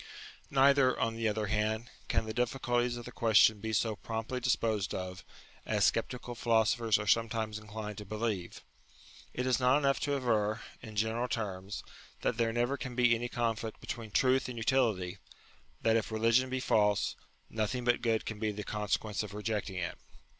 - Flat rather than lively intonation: Yes, narrow, 2.3 semitones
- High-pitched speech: No, low, 115 Hz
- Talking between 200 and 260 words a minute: No, average, 175 wpm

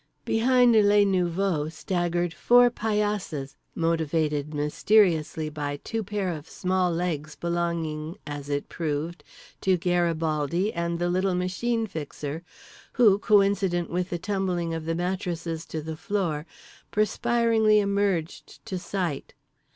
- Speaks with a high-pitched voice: No, medium, 175 Hz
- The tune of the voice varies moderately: Yes, average, 3.9 semitones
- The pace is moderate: No, slow, 120 wpm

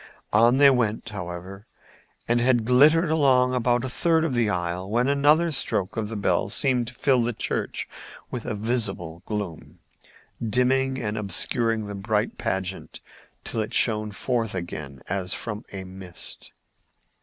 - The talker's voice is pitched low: Yes, low, 115 Hz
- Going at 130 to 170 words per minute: Yes, average, 155 wpm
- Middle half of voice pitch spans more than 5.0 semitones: No, average, 4.5 semitones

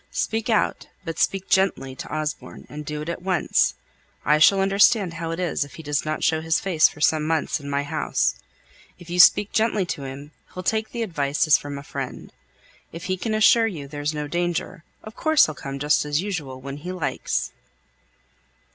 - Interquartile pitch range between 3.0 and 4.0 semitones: No, average, 4.5 semitones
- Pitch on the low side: No, medium, 160 Hz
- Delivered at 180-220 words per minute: Yes, average, 200 wpm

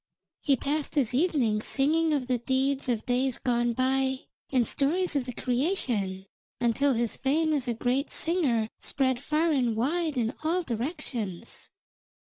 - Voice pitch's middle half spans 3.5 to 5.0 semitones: Yes, average, 3.8 semitones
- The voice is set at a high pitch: Yes, very high, 265 Hz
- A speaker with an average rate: Yes, average, 150 wpm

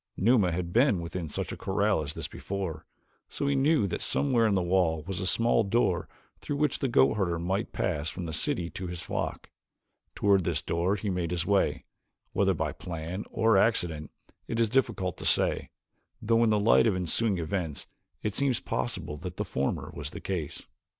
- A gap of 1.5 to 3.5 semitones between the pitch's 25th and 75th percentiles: No, average, 4.8 semitones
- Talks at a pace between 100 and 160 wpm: No, average, 195 wpm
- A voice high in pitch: No, very low, 95 Hz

